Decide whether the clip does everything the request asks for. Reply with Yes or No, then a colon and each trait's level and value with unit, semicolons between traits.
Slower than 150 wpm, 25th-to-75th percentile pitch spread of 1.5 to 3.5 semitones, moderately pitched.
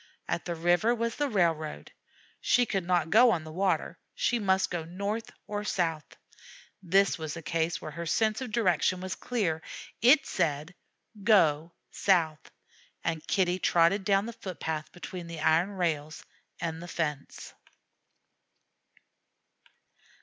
No: average, 140 wpm; average, 4.0 semitones; medium, 175 Hz